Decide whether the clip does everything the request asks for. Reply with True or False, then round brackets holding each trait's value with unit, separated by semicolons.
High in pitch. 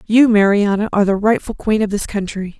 True (205 Hz)